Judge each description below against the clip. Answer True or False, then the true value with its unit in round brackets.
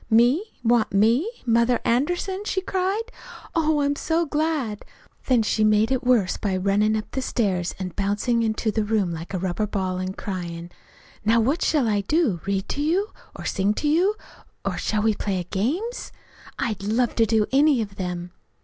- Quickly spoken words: False (180 wpm)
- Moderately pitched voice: False (225 Hz)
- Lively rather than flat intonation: True (6.6 semitones)